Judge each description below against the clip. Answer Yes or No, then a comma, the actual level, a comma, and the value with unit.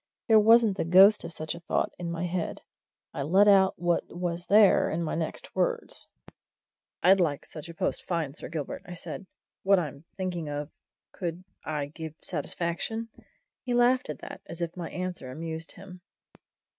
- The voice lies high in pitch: No, medium, 175 Hz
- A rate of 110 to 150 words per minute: No, average, 175 wpm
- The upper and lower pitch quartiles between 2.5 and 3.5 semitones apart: Yes, average, 3.0 semitones